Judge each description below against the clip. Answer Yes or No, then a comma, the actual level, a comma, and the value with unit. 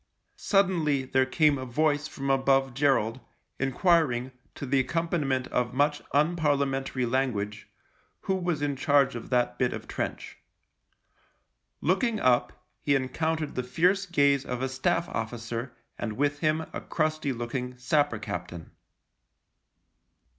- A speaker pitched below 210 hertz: Yes, low, 135 Hz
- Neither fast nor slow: No, slow, 130 wpm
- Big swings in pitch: No, average, 3.6 semitones